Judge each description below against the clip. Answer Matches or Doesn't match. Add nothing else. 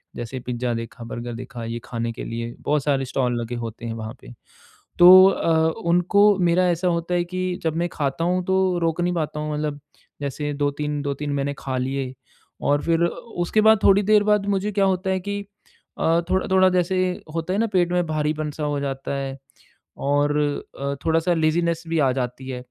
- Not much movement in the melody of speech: Doesn't match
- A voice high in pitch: Doesn't match